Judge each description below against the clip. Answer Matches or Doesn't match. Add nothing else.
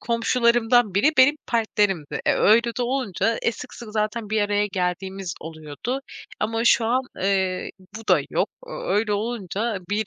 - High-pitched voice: Matches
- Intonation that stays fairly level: Doesn't match